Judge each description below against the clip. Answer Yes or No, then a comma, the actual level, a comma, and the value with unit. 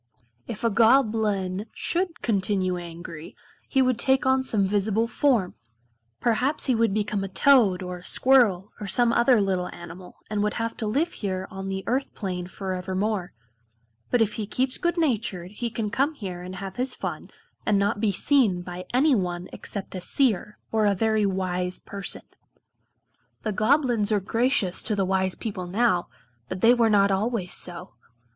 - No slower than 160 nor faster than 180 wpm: Yes, average, 170 wpm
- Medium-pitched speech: No, high, 210 Hz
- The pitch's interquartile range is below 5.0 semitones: Yes, average, 4.1 semitones